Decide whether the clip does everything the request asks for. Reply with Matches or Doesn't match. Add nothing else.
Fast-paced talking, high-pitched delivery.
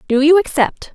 Doesn't match